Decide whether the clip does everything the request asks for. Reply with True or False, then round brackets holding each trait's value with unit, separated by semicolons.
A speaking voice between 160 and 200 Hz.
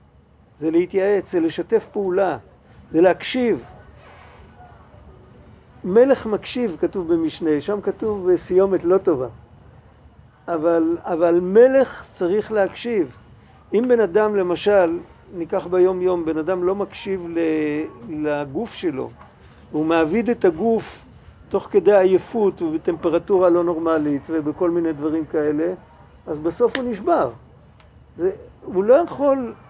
True (185 Hz)